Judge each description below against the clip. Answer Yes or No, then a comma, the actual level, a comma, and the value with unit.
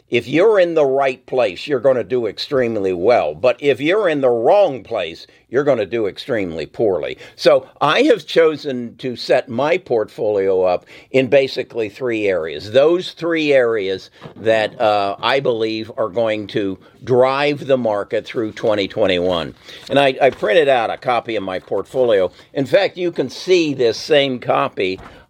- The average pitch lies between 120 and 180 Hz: Yes, medium, 140 Hz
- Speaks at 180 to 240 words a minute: No, average, 170 wpm